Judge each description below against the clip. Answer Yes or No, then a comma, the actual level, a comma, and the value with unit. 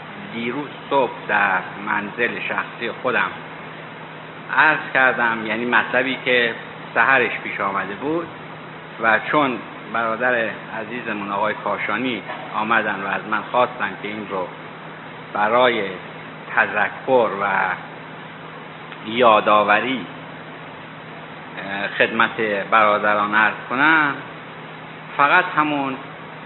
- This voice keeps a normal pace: No, slow, 90 wpm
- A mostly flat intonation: No, average, 4.8 semitones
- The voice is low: Yes, low, 115 Hz